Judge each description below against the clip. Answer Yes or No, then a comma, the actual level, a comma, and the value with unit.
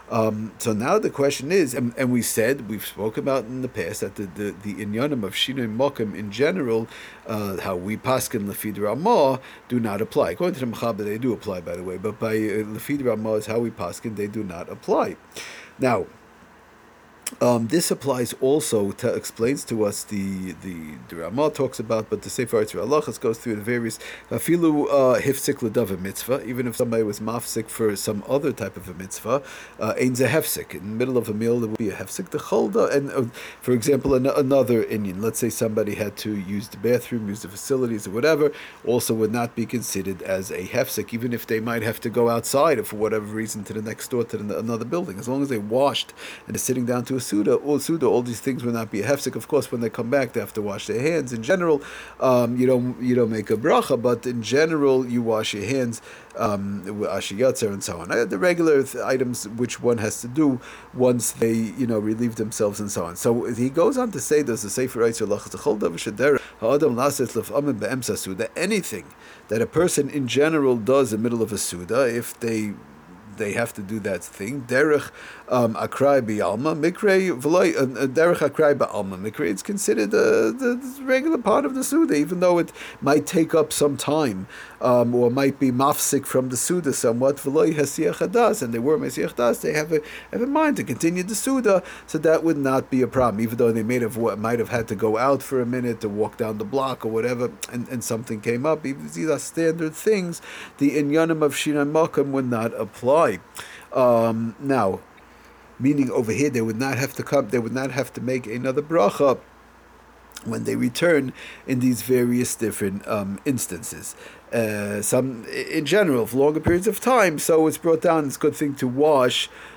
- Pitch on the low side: Yes, low, 125 Hz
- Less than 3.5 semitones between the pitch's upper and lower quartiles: No, average, 4.4 semitones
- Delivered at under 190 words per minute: No, average, 200 wpm